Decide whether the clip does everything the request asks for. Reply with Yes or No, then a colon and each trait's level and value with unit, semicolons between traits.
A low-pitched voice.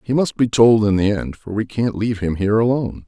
Yes: low, 110 Hz